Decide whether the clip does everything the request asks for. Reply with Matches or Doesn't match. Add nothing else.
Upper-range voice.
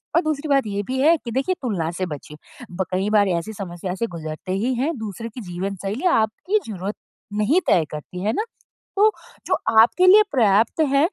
Matches